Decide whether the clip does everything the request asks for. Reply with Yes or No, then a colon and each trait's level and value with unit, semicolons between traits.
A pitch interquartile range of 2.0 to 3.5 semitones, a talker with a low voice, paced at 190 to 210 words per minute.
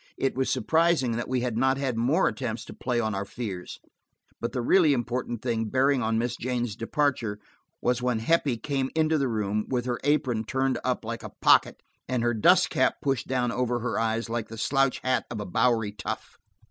Yes: average, 2.7 semitones; low, 120 Hz; fast, 205 wpm